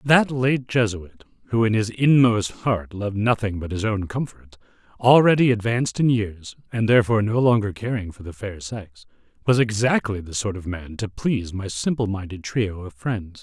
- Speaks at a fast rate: No, average, 180 wpm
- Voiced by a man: Yes, male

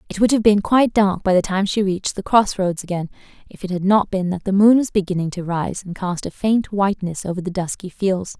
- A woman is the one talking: Yes, female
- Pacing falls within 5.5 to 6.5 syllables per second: Yes, 5.8 syllables/s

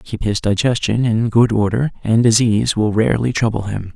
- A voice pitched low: Yes, low, 110 Hz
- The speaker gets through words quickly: No, average, 180 wpm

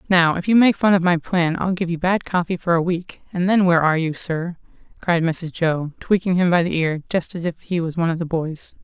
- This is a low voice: No, medium, 175 Hz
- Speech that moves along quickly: Yes, fast, 265 wpm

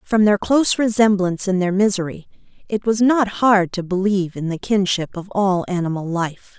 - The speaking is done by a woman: Yes, female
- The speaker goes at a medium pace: Yes, average, 180 wpm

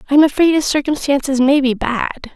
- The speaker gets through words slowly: No, fast, 205 wpm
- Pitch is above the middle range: Yes, very high, 280 Hz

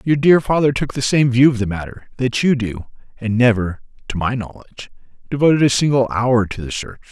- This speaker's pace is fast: Yes, fast, 210 wpm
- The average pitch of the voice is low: Yes, low, 120 Hz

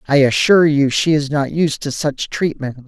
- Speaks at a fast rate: Yes, fast, 210 wpm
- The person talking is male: Yes, male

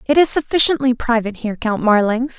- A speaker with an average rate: Yes, average, 175 wpm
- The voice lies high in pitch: Yes, high, 245 Hz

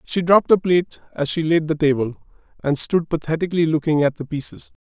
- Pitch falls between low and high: Yes, medium, 160 Hz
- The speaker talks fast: No, average, 195 wpm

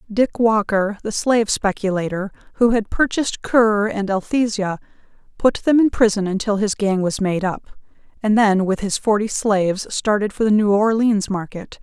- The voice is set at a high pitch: Yes, high, 210 Hz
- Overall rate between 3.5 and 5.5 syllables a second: Yes, 4.9 syllables/s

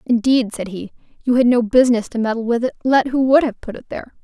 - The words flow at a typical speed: No, fast, 255 wpm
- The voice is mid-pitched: No, high, 240 Hz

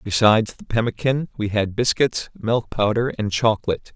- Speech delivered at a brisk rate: No, average, 150 wpm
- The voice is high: No, low, 115 Hz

